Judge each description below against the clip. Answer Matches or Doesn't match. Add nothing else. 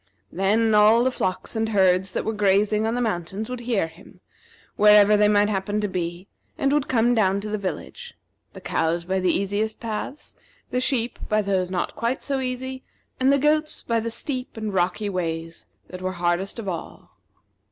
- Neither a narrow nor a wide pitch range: Matches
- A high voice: Matches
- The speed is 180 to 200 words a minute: Matches